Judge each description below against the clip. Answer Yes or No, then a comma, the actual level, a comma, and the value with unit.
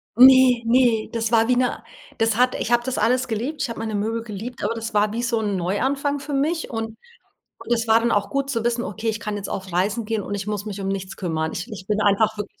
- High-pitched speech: Yes, high, 225 Hz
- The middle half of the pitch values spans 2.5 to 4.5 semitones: Yes, average, 2.9 semitones